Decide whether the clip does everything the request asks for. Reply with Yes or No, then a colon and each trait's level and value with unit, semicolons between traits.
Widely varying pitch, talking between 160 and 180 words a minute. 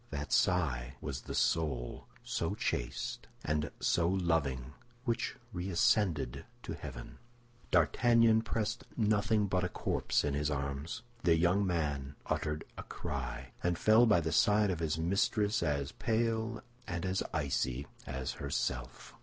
No: wide, 6.4 semitones; slow, 135 wpm